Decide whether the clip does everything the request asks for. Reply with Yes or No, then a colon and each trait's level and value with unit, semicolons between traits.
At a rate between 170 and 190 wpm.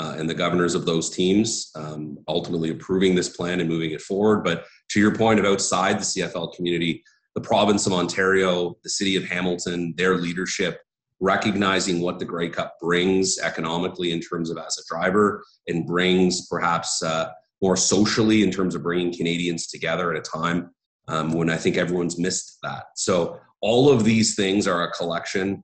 Yes: average, 185 wpm